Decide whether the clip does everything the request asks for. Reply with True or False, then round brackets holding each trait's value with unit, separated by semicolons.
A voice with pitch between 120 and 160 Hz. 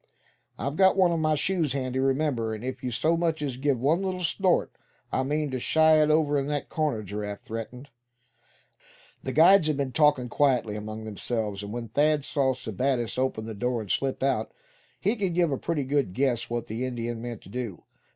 True (135 Hz)